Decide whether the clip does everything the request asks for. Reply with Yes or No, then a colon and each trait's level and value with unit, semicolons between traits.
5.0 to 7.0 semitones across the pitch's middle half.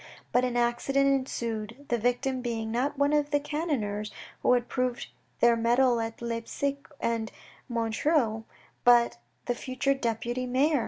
No: average, 3.0 semitones